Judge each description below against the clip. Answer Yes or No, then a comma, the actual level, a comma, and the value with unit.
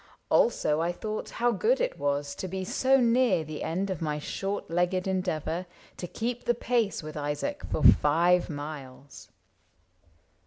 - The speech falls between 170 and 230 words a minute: No, average, 155 wpm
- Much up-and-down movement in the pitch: Yes, wide, 7.2 semitones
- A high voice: No, medium, 180 Hz